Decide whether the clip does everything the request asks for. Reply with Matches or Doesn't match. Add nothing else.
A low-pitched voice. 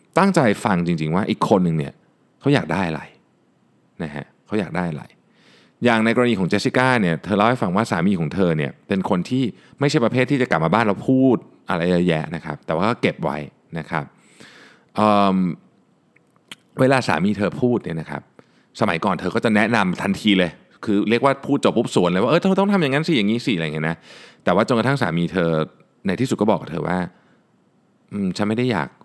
Matches